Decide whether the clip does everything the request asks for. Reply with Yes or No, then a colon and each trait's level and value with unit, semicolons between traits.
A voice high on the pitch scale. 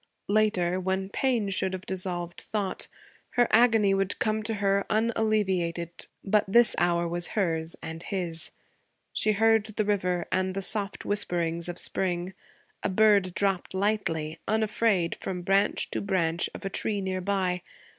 Yes: high, 195 Hz